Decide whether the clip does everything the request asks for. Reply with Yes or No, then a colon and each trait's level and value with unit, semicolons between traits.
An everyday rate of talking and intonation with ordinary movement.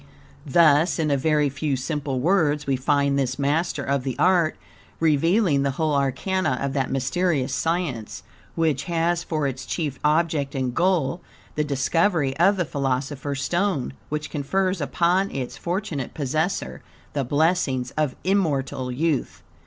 Yes: average, 145 wpm; average, 3.8 semitones